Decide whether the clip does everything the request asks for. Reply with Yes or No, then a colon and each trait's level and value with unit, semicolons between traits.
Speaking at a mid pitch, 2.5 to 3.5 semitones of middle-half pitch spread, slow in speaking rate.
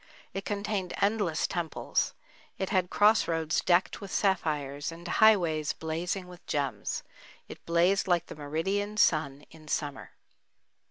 No: medium, 175 Hz; average, 4.0 semitones; slow, 130 wpm